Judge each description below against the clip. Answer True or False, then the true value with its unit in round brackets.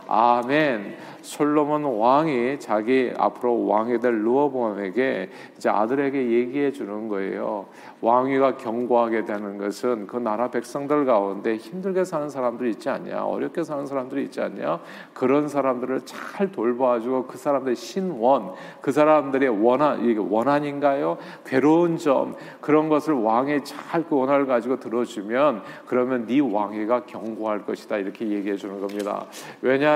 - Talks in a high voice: False (130 Hz)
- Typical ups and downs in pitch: True (4.1 semitones)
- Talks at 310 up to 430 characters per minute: True (315 characters per minute)